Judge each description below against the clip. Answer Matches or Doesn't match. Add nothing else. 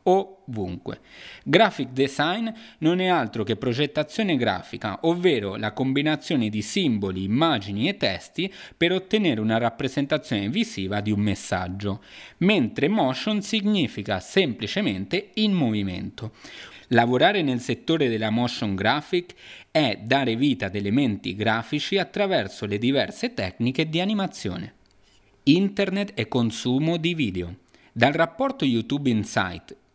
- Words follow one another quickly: Doesn't match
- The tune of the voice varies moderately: Doesn't match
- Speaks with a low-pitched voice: Matches